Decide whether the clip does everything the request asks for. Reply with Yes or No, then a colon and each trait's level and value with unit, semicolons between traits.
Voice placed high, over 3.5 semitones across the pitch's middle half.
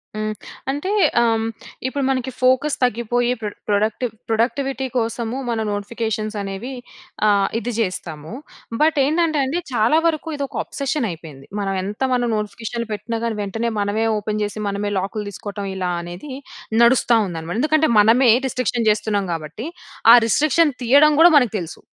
Yes: high, 225 Hz; average, 4.2 semitones